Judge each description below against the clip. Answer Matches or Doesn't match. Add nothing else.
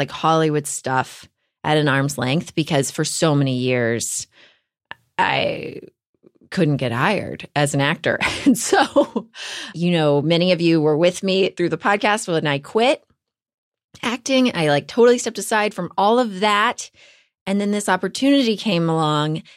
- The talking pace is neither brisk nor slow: Matches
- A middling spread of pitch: Doesn't match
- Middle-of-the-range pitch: Matches